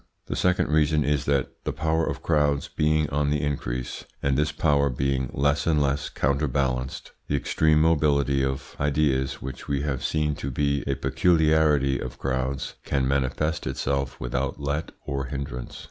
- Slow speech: No, average, 160 wpm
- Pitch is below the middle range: Yes, very low, 70 Hz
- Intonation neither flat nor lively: No, narrow, 2.1 semitones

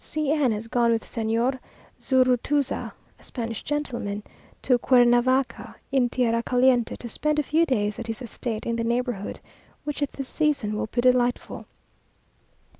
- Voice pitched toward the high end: Yes, high, 245 Hz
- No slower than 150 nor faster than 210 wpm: Yes, average, 155 wpm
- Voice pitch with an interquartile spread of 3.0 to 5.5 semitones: No, narrow, 2.6 semitones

